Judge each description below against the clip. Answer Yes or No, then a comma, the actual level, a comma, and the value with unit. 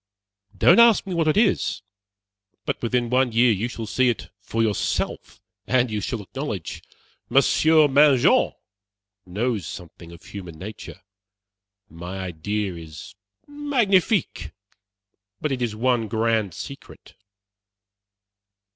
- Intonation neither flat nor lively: No, wide, 6.1 semitones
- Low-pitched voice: Yes, low, 115 Hz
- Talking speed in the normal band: No, slow, 120 wpm